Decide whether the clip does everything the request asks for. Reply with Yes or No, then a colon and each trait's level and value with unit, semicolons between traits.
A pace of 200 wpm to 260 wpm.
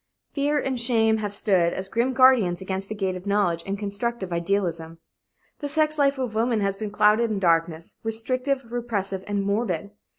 No: average, 175 wpm